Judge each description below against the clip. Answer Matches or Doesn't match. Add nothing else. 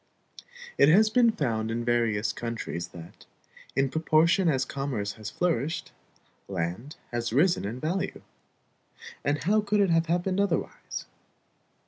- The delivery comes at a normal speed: Doesn't match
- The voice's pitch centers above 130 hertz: Matches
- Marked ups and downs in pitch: Matches